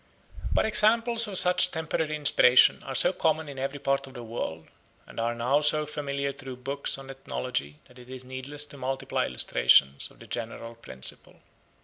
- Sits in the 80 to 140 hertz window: Yes, low, 135 Hz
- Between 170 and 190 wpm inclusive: Yes, average, 175 wpm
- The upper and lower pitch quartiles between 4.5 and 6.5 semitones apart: No, average, 3.2 semitones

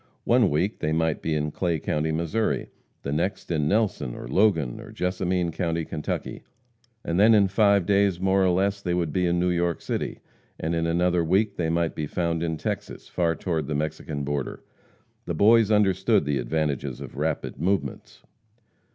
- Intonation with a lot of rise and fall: No, average, 3.6 semitones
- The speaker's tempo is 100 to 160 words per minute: No, average, 185 wpm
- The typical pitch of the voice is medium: No, very low, 85 Hz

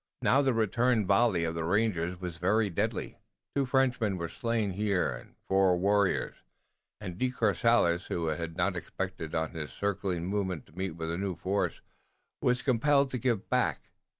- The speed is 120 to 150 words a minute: No, average, 170 wpm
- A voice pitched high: No, very low, 95 Hz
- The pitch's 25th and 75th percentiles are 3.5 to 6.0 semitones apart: Yes, average, 5.1 semitones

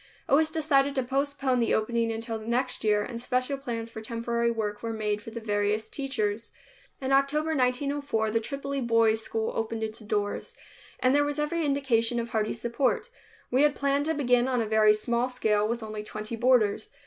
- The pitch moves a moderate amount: Yes, average, 3.8 semitones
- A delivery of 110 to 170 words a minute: No, average, 195 wpm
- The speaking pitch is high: Yes, high, 235 Hz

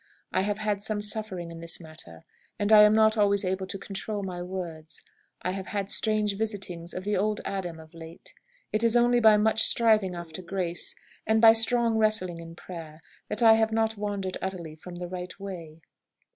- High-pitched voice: Yes, high, 195 Hz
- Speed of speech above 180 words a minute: Yes, average, 190 wpm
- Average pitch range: Yes, average, 3.6 semitones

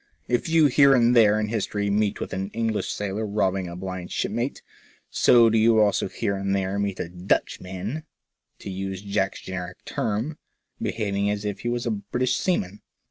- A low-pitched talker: Yes, low, 105 Hz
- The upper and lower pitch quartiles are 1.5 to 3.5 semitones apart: Yes, average, 3.2 semitones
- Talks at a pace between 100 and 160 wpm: No, average, 185 wpm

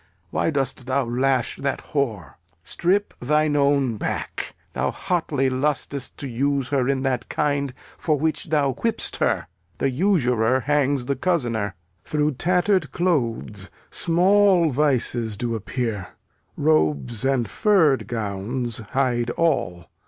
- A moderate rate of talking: No, slow, 125 wpm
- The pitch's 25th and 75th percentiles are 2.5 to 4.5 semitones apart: Yes, average, 4.1 semitones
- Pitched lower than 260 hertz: Yes, low, 135 Hz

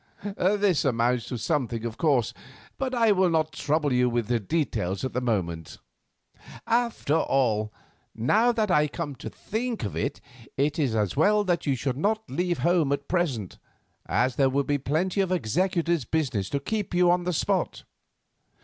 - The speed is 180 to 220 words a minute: No, average, 170 wpm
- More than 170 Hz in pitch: No, medium, 150 Hz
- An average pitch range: No, wide, 6.7 semitones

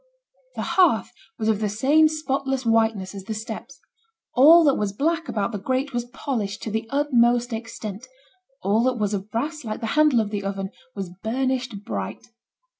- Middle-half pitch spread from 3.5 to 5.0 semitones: Yes, average, 4.4 semitones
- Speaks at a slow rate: No, average, 180 wpm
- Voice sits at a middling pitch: No, high, 230 Hz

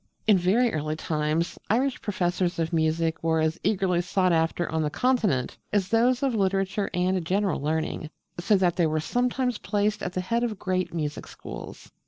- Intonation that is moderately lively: Yes, average, 4.3 semitones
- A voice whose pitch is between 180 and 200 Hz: Yes, medium, 185 Hz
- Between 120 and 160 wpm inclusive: No, average, 180 wpm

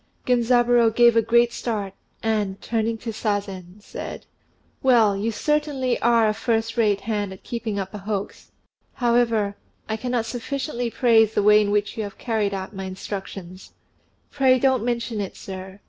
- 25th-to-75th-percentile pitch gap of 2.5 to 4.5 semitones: Yes, average, 2.8 semitones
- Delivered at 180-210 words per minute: No, average, 160 wpm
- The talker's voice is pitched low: No, high, 225 Hz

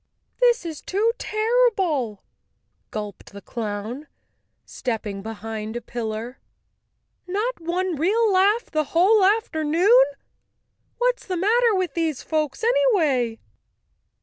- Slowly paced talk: Yes, slow, 115 wpm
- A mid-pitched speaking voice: No, very high, 335 Hz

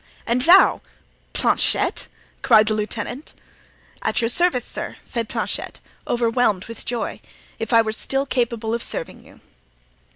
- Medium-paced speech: No, slow, 130 wpm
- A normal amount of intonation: No, narrow, 2.0 semitones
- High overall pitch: Yes, high, 235 Hz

